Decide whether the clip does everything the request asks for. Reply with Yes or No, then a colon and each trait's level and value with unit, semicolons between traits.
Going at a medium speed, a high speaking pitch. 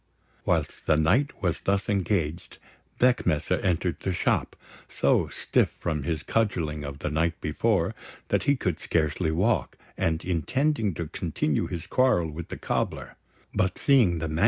No: average, 155 wpm; very low, 85 Hz